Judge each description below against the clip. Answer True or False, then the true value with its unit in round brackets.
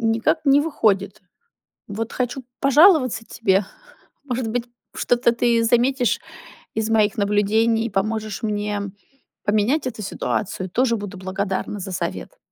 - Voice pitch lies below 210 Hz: False (225 Hz)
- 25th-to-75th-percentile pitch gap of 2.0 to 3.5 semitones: True (3.1 semitones)